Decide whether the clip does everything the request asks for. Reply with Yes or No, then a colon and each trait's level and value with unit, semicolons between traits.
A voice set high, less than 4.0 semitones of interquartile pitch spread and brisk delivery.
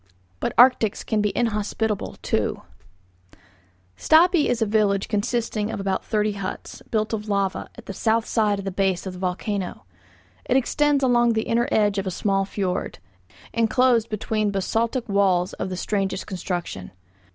No: high, 210 Hz; average, 2.8 semitones; average, 160 wpm